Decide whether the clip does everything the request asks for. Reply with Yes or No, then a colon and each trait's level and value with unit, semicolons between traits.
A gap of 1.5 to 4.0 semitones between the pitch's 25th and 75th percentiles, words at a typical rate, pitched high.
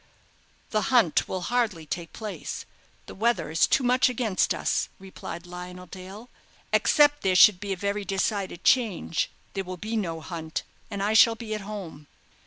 Yes: average, 3.7 semitones; average, 170 wpm; high, 195 Hz